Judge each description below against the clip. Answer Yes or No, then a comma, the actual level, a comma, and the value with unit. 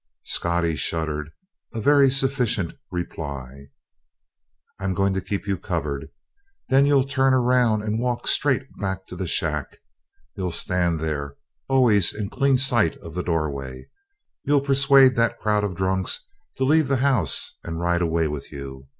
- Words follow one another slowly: No, average, 155 wpm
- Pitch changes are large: Yes, wide, 8.0 semitones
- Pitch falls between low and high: No, very low, 95 Hz